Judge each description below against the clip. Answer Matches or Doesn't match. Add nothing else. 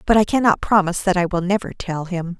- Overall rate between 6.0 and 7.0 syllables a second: Matches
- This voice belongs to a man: Doesn't match